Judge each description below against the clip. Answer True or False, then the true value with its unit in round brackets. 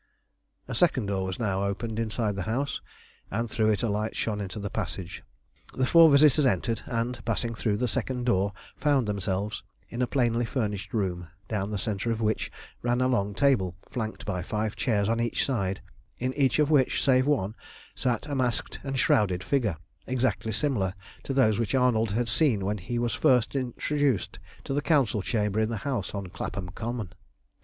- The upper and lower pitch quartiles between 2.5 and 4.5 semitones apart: True (4.0 semitones)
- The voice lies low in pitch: True (115 Hz)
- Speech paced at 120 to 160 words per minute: False (185 wpm)